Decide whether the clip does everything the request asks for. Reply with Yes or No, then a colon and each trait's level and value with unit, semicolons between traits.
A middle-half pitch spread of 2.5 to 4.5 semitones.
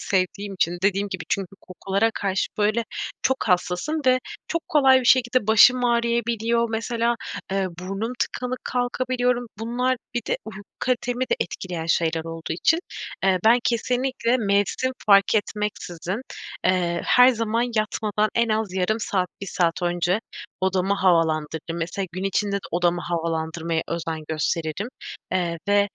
No: average, 5.0 semitones